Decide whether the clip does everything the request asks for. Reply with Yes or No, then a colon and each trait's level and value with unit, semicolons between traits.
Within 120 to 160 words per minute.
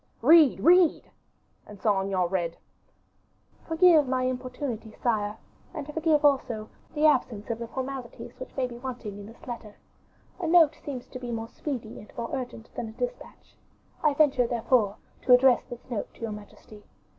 No: average, 170 wpm